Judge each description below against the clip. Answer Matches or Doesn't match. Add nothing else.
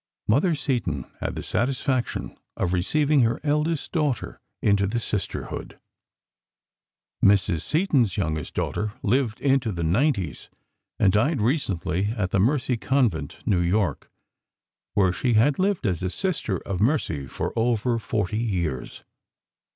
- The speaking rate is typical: Doesn't match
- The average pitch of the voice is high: Doesn't match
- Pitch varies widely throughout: Matches